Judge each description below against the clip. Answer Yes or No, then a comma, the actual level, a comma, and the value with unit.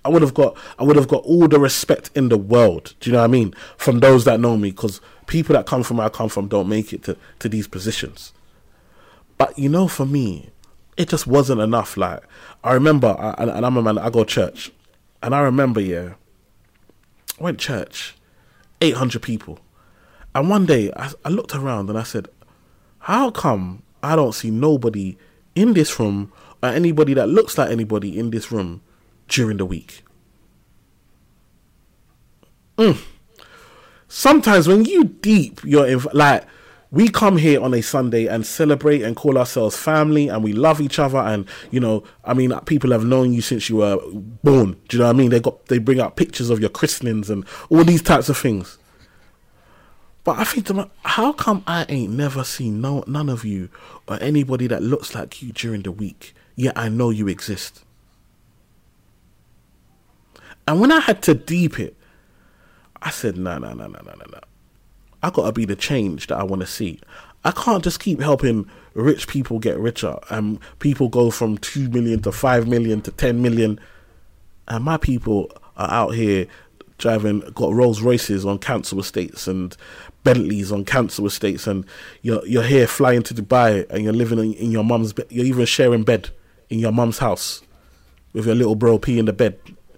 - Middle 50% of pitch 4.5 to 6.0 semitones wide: Yes, average, 4.8 semitones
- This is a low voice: Yes, low, 115 Hz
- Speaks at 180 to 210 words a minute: Yes, average, 190 wpm